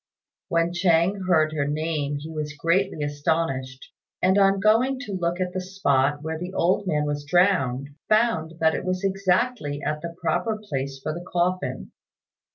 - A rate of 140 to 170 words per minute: Yes, average, 165 wpm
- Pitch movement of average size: Yes, average, 4.2 semitones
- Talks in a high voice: No, medium, 170 Hz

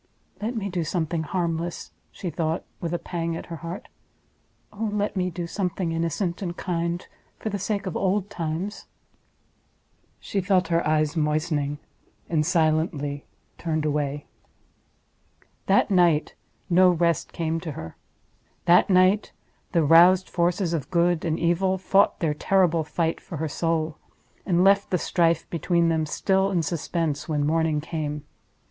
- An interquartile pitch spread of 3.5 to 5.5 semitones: No, narrow, 2.6 semitones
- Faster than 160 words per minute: No, average, 145 wpm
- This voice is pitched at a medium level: Yes, medium, 170 Hz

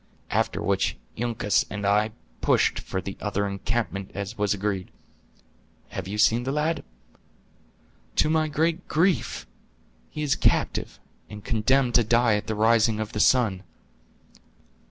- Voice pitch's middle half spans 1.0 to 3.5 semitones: No, average, 4.1 semitones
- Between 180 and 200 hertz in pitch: No, low, 110 Hz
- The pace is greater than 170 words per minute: No, average, 140 wpm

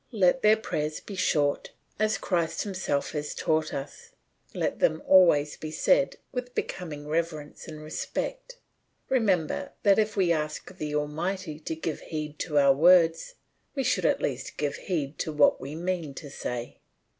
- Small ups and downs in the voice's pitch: No, average, 4.2 semitones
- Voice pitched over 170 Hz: No, medium, 160 Hz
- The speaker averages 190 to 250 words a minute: No, average, 160 wpm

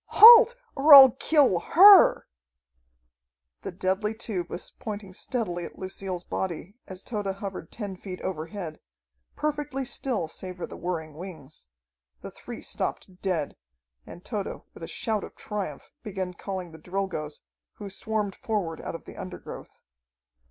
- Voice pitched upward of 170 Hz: Yes, high, 190 Hz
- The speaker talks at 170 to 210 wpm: No, average, 145 wpm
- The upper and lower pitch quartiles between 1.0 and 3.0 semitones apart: No, average, 3.8 semitones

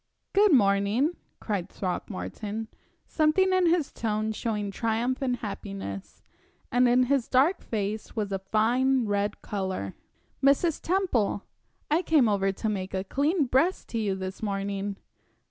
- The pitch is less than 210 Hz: No, high, 220 Hz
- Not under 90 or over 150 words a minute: Yes, average, 140 wpm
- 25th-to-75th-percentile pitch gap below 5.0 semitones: No, average, 5.3 semitones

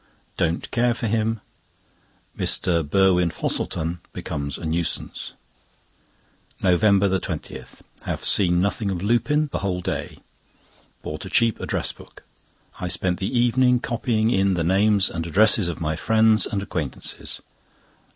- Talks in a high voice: No, very low, 95 Hz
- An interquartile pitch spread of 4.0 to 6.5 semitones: Yes, average, 4.3 semitones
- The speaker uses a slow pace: Yes, slow, 130 wpm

